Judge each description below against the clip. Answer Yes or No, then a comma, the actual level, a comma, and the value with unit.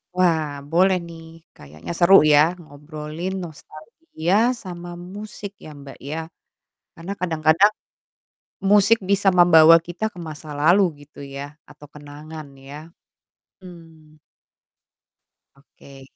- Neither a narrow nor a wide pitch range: Yes, average, 3.2 semitones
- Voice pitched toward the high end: No, medium, 160 Hz